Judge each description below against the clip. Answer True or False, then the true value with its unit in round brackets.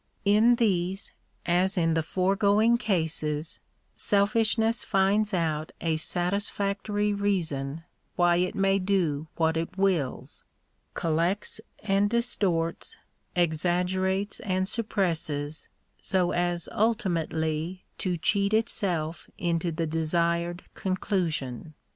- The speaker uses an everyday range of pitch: True (3.5 semitones)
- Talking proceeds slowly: True (105 wpm)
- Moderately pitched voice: True (180 Hz)